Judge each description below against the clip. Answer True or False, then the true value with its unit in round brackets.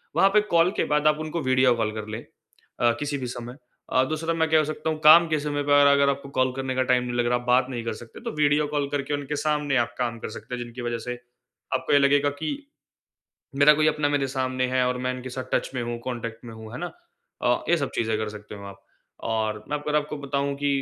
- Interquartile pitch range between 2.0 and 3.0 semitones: False (3.4 semitones)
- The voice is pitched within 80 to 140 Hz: True (135 Hz)